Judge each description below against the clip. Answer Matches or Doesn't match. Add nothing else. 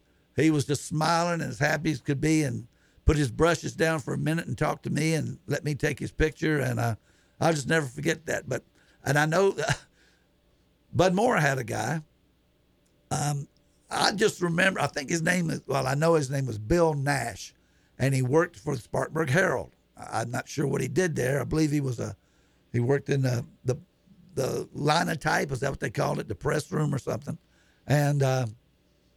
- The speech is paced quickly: Matches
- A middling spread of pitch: Matches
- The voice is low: Doesn't match